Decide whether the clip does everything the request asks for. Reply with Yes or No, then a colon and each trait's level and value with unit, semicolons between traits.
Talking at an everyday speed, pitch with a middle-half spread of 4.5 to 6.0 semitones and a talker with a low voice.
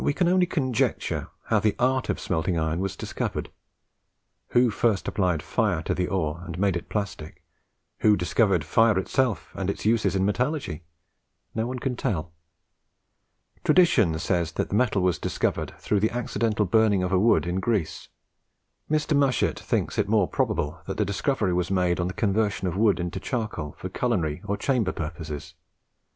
Yes: average, 170 wpm; average, 4.8 semitones; low, 100 Hz